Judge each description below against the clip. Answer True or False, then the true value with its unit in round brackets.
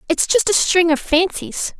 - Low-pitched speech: False (360 Hz)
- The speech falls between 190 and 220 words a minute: True (200 wpm)